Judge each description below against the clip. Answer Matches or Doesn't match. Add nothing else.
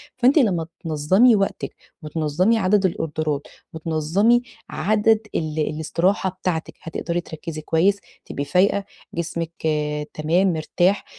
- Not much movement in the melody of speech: Doesn't match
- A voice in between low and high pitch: Matches